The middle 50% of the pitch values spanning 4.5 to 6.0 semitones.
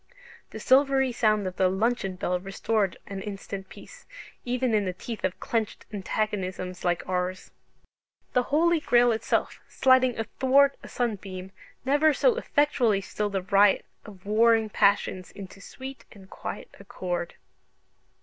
Yes: average, 4.9 semitones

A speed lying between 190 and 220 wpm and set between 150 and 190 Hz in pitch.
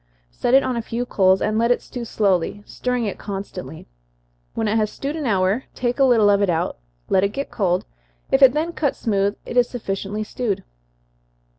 No: average, 200 wpm; high, 215 Hz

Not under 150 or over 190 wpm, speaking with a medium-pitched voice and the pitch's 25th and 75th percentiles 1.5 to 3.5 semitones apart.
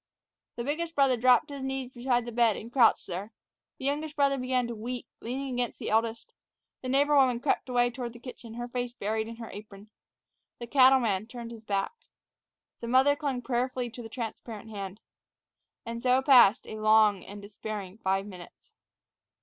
No: average, 180 wpm; high, 240 Hz; average, 2.9 semitones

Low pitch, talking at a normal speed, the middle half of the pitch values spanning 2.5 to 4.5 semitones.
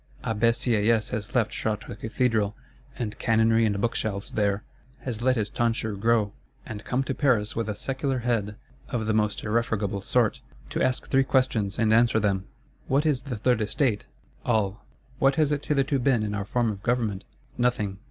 Yes: low, 115 Hz; average, 175 wpm; average, 3.0 semitones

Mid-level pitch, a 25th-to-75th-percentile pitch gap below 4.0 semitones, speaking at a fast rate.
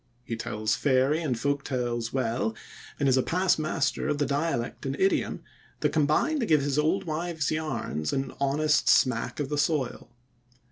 No: medium, 145 Hz; average, 3.4 semitones; average, 175 wpm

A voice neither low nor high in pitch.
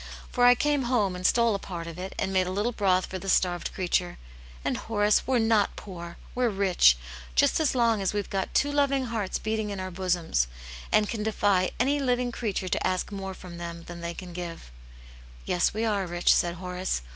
No: high, 195 Hz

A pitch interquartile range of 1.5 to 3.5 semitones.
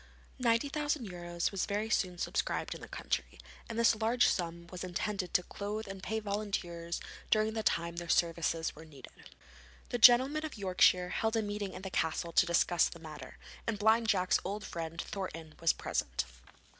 No: average, 4.3 semitones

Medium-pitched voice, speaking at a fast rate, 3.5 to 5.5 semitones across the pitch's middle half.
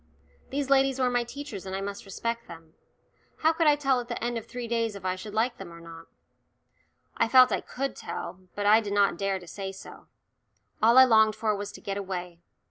No: high, 220 Hz; fast, 225 wpm; average, 4.2 semitones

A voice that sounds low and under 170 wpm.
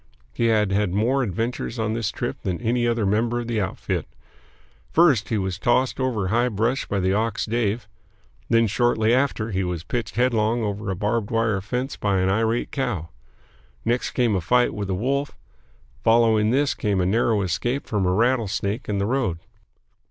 No: low, 110 Hz; average, 185 wpm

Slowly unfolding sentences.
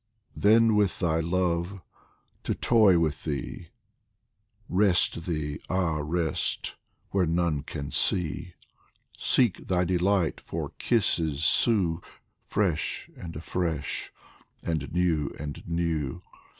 Yes: slow, 105 wpm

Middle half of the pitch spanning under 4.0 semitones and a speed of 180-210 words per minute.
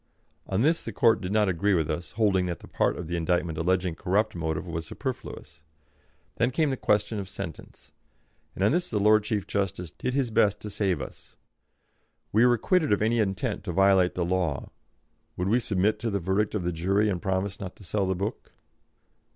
Yes: average, 3.2 semitones; fast, 205 wpm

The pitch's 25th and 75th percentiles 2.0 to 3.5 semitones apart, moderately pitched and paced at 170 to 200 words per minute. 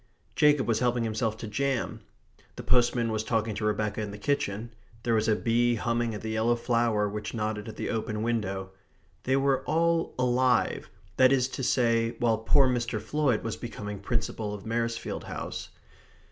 No: narrow, 2.4 semitones; low, 115 Hz; average, 175 wpm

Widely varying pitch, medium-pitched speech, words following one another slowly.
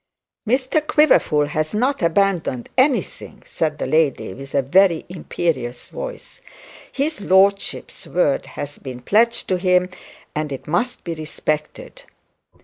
Yes: wide, 7.6 semitones; medium, 175 Hz; slow, 130 wpm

